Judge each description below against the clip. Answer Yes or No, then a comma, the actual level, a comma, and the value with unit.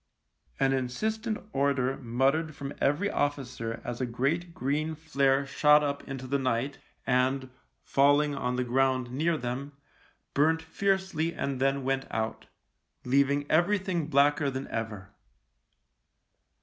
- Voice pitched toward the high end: No, medium, 140 Hz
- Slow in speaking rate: Yes, slow, 125 wpm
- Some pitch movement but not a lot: Yes, average, 3.1 semitones